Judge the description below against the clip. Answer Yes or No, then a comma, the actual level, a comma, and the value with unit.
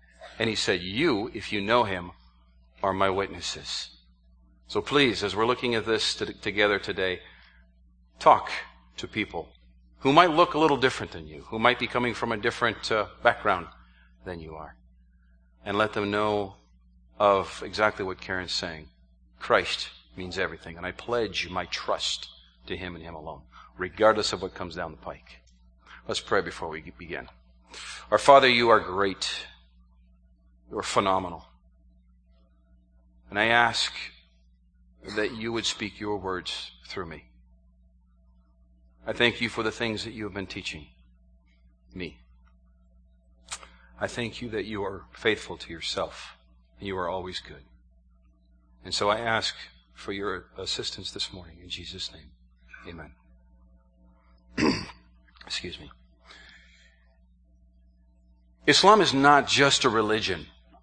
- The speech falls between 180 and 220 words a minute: No, average, 140 wpm